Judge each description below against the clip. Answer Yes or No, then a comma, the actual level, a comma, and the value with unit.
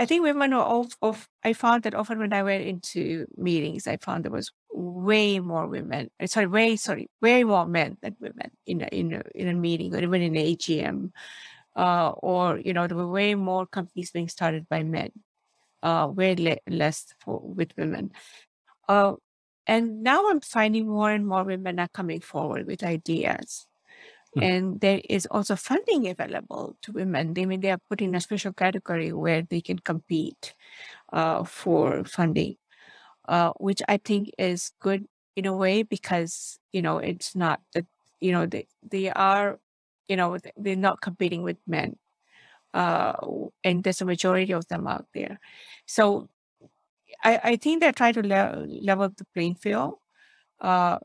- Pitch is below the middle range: No, high, 190 Hz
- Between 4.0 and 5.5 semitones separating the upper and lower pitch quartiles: No, average, 3.4 semitones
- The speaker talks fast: No, average, 175 wpm